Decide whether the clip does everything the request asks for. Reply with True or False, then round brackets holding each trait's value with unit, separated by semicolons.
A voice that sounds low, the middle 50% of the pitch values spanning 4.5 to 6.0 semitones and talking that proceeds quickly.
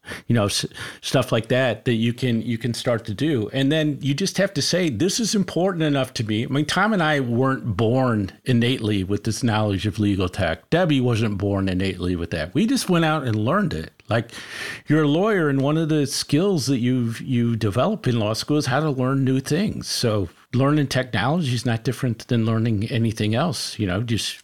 True (125 Hz; 5.1 semitones; 220 wpm)